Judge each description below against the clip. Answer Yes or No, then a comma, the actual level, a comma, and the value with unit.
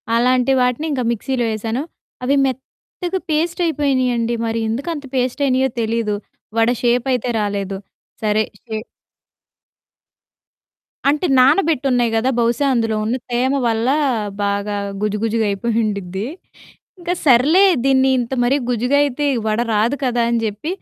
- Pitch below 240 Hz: No, high, 245 Hz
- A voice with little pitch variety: No, average, 3.2 semitones